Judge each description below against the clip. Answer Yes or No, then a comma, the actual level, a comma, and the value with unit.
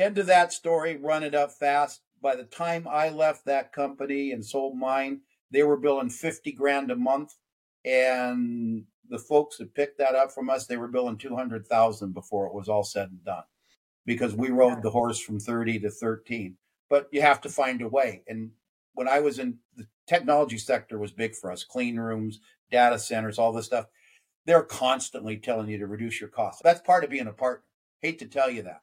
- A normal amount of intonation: Yes, average, 4.2 semitones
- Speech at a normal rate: No, fast, 210 wpm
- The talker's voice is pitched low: Yes, low, 125 Hz